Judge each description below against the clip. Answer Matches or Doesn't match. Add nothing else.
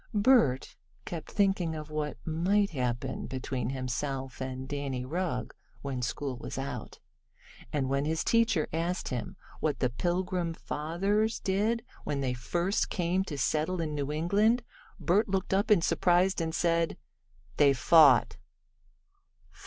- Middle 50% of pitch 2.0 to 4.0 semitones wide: Doesn't match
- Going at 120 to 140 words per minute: Matches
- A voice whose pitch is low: Doesn't match